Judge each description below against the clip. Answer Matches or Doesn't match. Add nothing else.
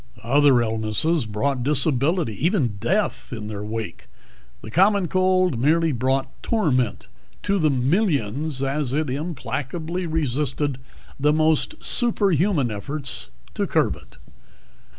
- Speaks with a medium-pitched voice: Matches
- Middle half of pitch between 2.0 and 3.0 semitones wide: Doesn't match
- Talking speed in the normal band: Doesn't match